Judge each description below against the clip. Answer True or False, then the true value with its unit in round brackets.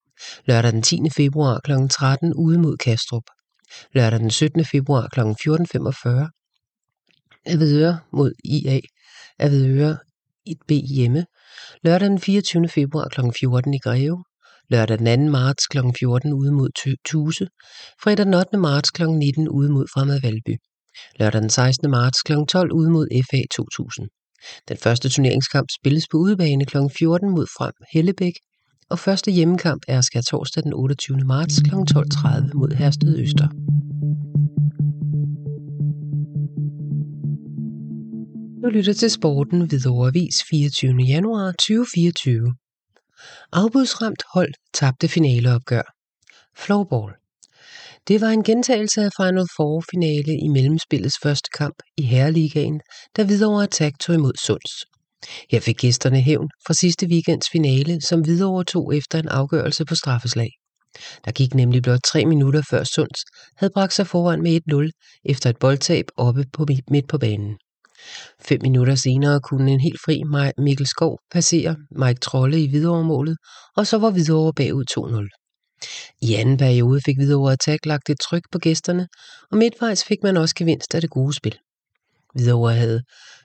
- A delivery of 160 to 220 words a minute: False (140 wpm)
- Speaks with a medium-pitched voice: True (150 Hz)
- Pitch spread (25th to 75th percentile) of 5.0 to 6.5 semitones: False (3.8 semitones)